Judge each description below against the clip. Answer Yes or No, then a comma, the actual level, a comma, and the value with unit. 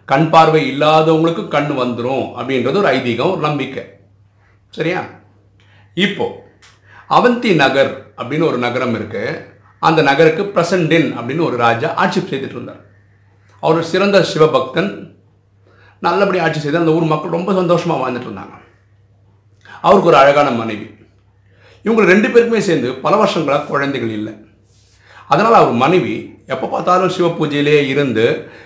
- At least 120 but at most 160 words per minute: No, average, 105 wpm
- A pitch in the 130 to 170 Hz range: Yes, low, 135 Hz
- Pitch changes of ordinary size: No, wide, 8.3 semitones